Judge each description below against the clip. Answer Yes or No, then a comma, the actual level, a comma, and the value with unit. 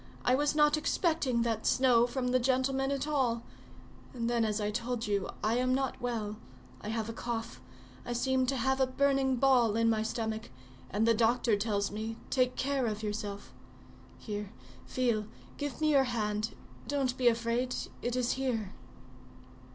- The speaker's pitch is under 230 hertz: No, high, 240 Hz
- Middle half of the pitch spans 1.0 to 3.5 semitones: Yes, average, 2.9 semitones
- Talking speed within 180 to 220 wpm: No, average, 165 wpm